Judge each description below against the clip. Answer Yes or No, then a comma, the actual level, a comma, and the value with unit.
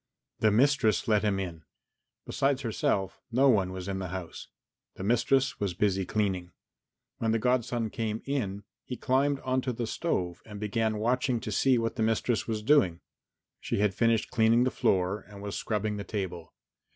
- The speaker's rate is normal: Yes, average, 175 wpm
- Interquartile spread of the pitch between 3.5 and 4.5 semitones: Yes, average, 3.9 semitones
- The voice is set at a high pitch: No, low, 110 Hz